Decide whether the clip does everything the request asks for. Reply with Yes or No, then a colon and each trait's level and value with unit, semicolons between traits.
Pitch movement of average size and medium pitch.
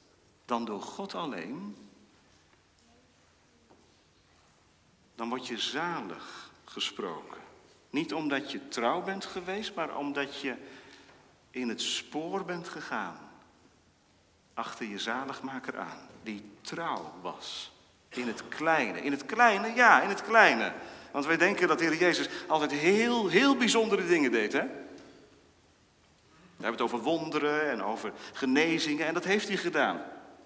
No: wide, 6.9 semitones; medium, 160 Hz